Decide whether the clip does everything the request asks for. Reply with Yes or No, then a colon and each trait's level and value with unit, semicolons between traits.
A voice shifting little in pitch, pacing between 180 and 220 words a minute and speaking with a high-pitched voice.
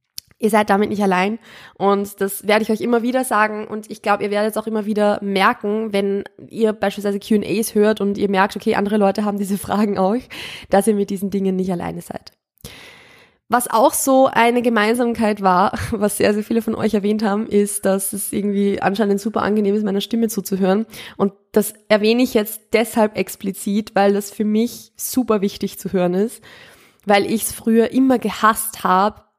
Yes: narrow, 1.7 semitones; fast, 190 wpm; high, 210 Hz